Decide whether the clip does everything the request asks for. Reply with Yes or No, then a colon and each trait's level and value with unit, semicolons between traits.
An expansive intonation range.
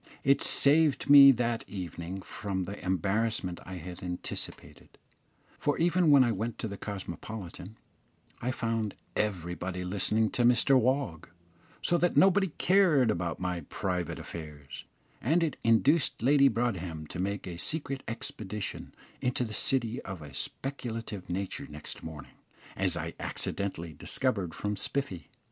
Yes: wide, 6.3 semitones